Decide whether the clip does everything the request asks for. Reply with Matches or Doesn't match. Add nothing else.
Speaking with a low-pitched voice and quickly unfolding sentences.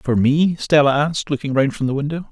Doesn't match